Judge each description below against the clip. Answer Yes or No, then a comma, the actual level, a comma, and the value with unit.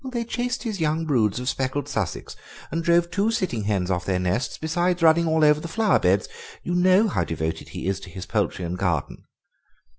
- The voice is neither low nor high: Yes, medium, 150 Hz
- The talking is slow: No, fast, 205 wpm